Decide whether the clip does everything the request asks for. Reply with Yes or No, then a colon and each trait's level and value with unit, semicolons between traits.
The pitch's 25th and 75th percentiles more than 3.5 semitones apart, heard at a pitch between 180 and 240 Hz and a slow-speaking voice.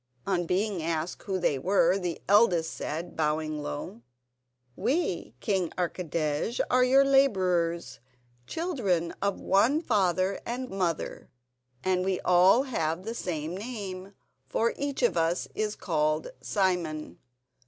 Yes: average, 4.5 semitones; medium, 185 Hz; slow, 125 wpm